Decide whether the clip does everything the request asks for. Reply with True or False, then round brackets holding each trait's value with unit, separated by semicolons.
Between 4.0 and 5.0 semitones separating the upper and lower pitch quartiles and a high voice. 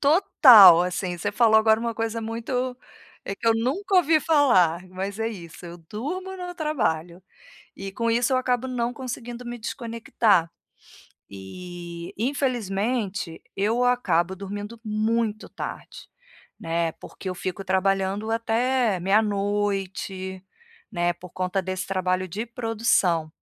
True (4.4 semitones; 210 Hz)